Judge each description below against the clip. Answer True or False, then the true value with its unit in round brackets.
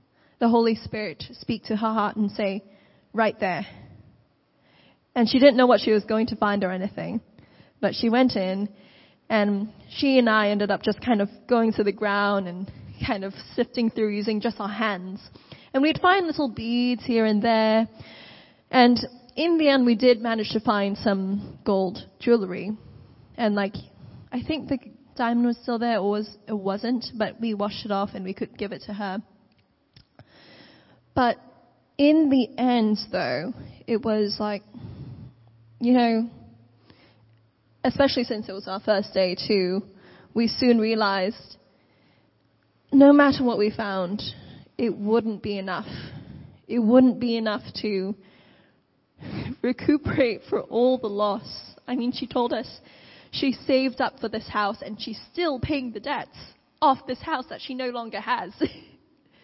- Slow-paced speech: False (160 wpm)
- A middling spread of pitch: True (3.4 semitones)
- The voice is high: True (220 Hz)